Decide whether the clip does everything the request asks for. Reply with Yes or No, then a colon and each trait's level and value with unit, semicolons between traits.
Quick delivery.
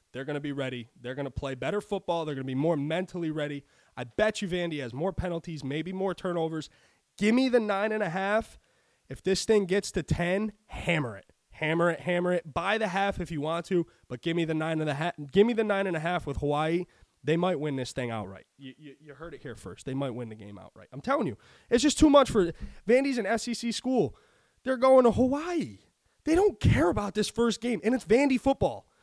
Yes: fast, 240 wpm